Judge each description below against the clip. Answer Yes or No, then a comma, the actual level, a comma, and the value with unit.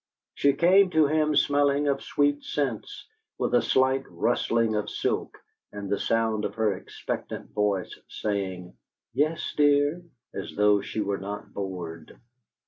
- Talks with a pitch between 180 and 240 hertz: No, low, 115 Hz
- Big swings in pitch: Yes, wide, 6.0 semitones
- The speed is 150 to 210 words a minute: No, average, 140 wpm